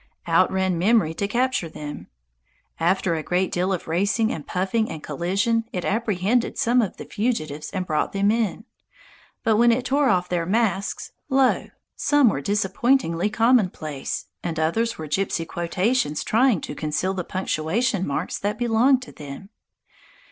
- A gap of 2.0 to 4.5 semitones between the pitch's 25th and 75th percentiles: No, wide, 5.4 semitones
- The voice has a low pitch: No, high, 195 Hz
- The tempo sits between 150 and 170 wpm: Yes, average, 155 wpm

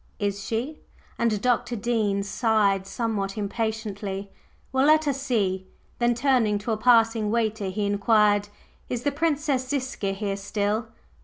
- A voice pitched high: Yes, high, 220 Hz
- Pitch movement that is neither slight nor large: Yes, average, 3.3 semitones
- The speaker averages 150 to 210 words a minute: No, average, 140 wpm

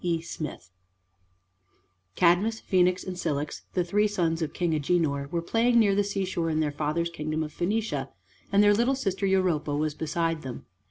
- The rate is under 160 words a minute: No, average, 170 wpm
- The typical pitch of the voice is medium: Yes, medium, 170 Hz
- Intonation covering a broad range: No, average, 4.1 semitones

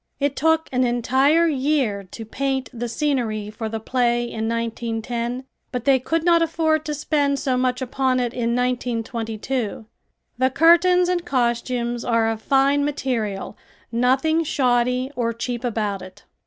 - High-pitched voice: Yes, very high, 250 Hz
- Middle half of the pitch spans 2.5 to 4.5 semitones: Yes, average, 3.3 semitones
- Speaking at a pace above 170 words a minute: No, average, 150 wpm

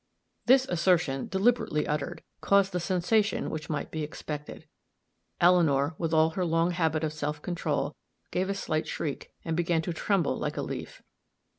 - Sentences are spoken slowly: No, average, 165 wpm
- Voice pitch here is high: No, medium, 165 Hz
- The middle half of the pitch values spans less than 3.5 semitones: Yes, average, 2.9 semitones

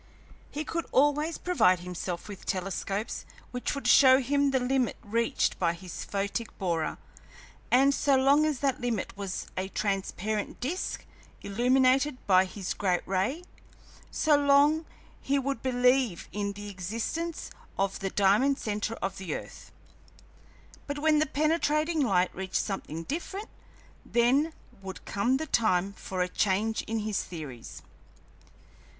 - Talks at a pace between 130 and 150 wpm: Yes, average, 140 wpm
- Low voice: No, high, 230 Hz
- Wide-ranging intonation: Yes, wide, 6.5 semitones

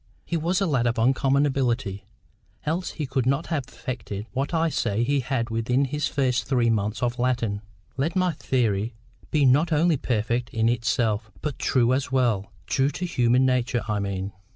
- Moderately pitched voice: No, low, 125 Hz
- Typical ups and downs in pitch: Yes, average, 3.6 semitones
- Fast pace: No, average, 175 wpm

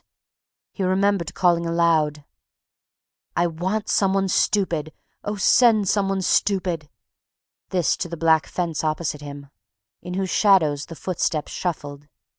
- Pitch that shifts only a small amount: No, average, 3.6 semitones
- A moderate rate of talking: No, slow, 130 wpm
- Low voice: No, medium, 175 Hz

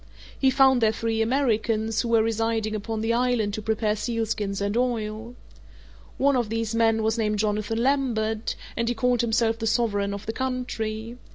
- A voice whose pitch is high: Yes, high, 225 Hz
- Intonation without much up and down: Yes, narrow, 1.7 semitones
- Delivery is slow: No, average, 175 wpm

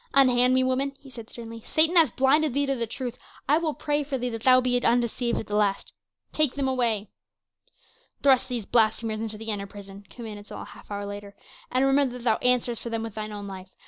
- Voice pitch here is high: Yes, high, 240 Hz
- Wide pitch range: No, average, 3.6 semitones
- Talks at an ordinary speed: No, fast, 225 wpm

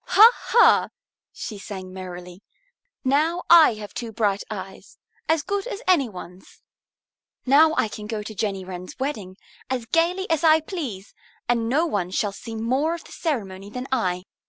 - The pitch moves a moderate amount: No, wide, 8.3 semitones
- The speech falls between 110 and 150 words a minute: No, average, 165 wpm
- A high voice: Yes, high, 230 Hz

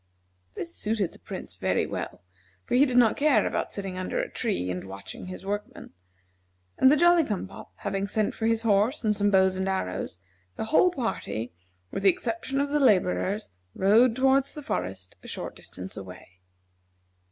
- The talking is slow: No, average, 180 wpm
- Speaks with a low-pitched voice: No, high, 205 Hz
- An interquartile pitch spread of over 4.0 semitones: Yes, wide, 5.5 semitones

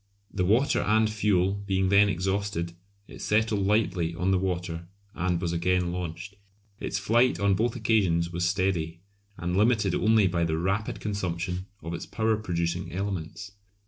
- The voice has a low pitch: Yes, very low, 95 Hz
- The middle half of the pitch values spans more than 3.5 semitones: No, average, 3.1 semitones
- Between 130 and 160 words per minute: Yes, average, 155 wpm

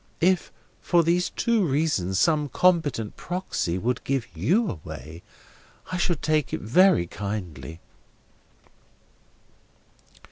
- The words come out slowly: Yes, slow, 105 wpm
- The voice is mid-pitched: Yes, medium, 145 Hz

